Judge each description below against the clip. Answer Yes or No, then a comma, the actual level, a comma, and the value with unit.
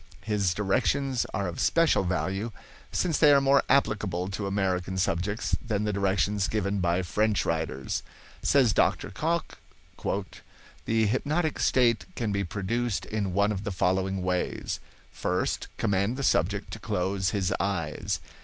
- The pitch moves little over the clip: No, average, 3.7 semitones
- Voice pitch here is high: No, low, 100 Hz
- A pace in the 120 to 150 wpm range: Yes, average, 145 wpm